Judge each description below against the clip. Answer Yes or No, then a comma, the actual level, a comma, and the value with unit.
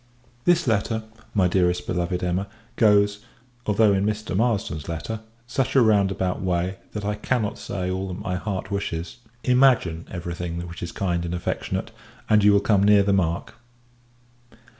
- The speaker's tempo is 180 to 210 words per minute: No, average, 160 wpm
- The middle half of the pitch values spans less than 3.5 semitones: Yes, average, 3.0 semitones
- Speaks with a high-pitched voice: No, low, 100 Hz